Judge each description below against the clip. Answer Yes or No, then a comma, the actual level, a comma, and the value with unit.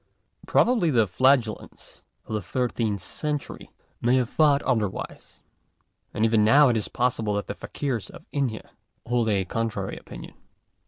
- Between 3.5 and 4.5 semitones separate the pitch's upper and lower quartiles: Yes, average, 3.8 semitones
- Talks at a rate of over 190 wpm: No, average, 145 wpm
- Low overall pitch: Yes, low, 115 Hz